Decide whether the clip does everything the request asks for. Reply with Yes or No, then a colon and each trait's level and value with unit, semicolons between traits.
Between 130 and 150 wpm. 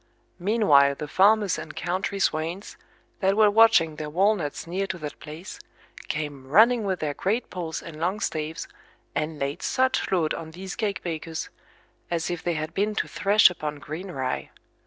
No: average, 170 wpm